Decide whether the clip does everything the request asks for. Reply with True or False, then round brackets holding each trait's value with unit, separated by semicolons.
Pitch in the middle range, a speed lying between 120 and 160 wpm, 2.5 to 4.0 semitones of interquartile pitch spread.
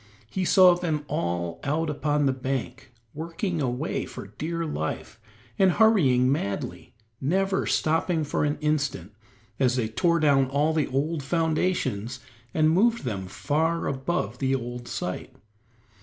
False (145 Hz; 135 wpm; 4.6 semitones)